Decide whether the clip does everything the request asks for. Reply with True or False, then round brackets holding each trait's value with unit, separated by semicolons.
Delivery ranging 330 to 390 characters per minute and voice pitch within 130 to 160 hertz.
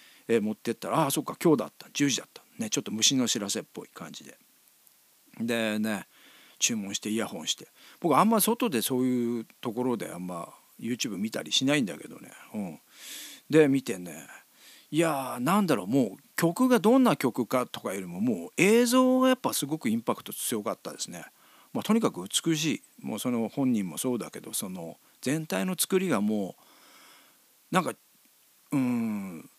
True (355 characters per minute; 135 Hz)